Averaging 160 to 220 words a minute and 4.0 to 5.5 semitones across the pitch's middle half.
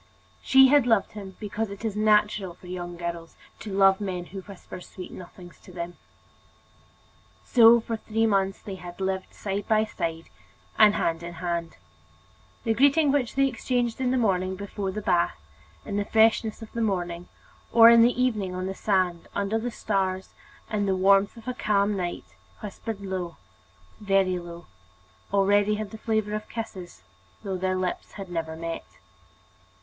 No: average, 170 wpm; average, 3.2 semitones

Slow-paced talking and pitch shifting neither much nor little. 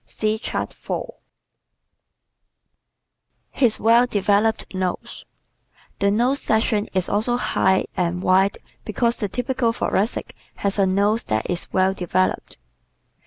Yes: slow, 120 wpm; average, 3.4 semitones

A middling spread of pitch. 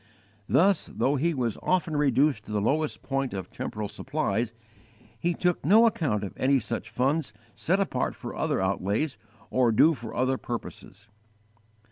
No: wide, 6.4 semitones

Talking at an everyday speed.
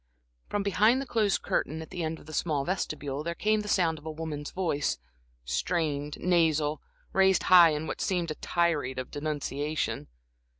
Yes: average, 175 wpm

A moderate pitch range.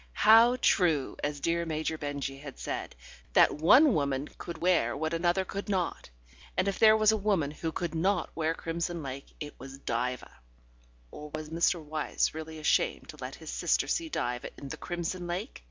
Yes: average, 3.9 semitones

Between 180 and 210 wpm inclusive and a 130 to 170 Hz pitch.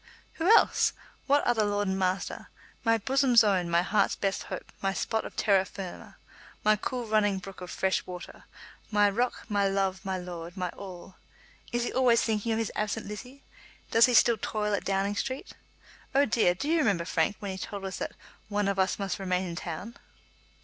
No: average, 195 wpm; high, 205 Hz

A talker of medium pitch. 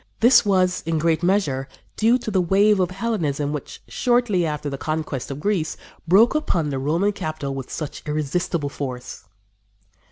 Yes: medium, 165 Hz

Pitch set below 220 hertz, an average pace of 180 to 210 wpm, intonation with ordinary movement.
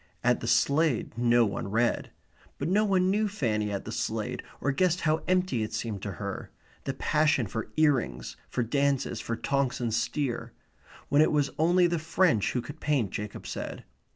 No: medium, 140 Hz; average, 185 wpm; wide, 5.8 semitones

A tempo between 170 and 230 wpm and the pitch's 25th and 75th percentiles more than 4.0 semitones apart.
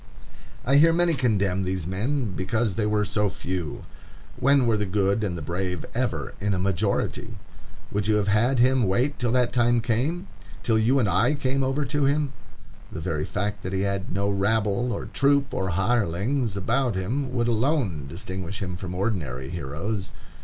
Yes: average, 175 wpm; average, 5.1 semitones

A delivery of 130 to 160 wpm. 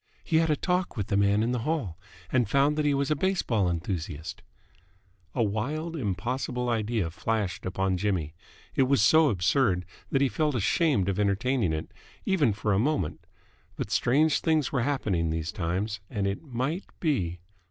No: average, 175 wpm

